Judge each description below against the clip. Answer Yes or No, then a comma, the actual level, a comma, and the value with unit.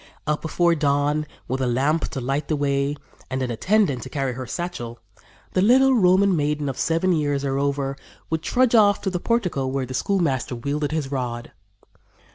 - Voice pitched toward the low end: No, medium, 145 Hz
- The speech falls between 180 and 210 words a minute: Yes, average, 185 wpm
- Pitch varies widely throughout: No, average, 4.6 semitones